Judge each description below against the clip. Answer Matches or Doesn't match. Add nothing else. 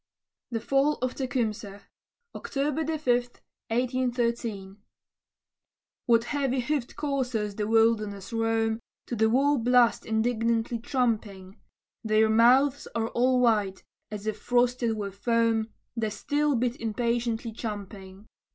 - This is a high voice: Matches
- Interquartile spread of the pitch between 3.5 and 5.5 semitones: Doesn't match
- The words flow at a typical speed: Doesn't match